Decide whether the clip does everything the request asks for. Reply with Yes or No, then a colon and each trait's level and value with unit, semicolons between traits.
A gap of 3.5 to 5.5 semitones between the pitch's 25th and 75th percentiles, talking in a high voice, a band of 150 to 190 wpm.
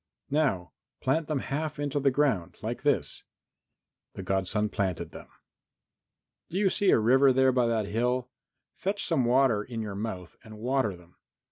No: average, 5.1 semitones; low, 125 Hz; average, 160 wpm